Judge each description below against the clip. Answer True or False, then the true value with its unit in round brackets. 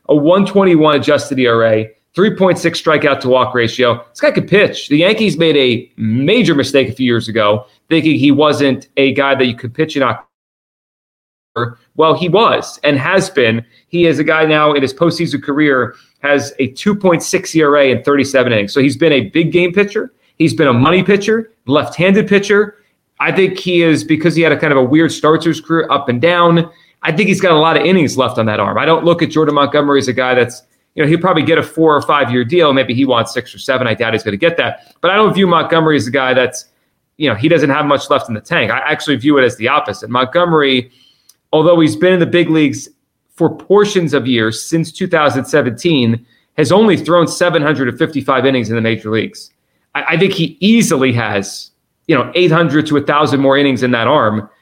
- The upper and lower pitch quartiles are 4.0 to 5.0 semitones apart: True (4.7 semitones)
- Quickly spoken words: True (220 wpm)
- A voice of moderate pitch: True (150 Hz)